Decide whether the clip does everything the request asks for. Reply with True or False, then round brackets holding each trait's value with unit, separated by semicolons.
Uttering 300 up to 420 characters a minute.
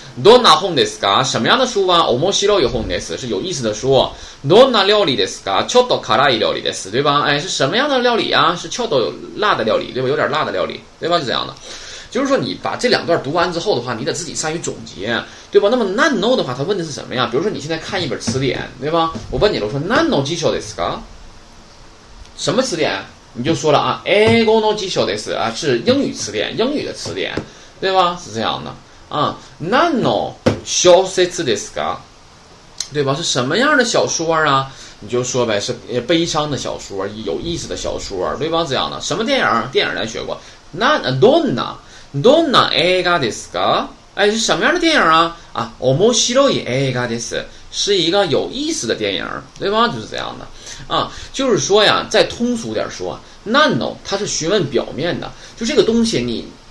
True (340 characters per minute)